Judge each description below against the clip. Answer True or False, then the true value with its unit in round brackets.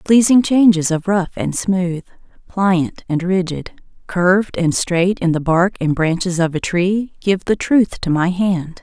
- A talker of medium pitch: True (180 Hz)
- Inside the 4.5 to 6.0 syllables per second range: False (4.2 syllables/s)